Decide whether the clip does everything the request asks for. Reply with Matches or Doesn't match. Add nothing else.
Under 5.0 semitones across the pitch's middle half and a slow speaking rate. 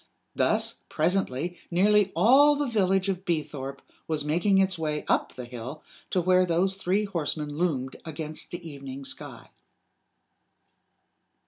Matches